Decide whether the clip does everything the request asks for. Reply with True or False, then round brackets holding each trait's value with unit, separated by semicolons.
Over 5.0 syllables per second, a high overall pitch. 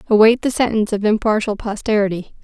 True (6.5 syllables/s; 215 Hz)